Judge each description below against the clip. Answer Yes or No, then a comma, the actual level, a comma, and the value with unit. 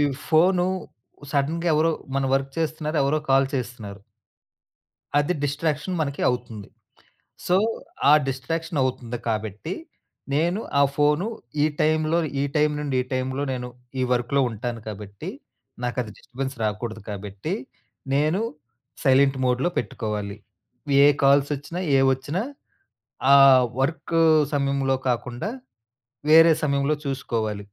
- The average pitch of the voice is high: No, low, 135 Hz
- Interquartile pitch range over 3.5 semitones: Yes, average, 4.0 semitones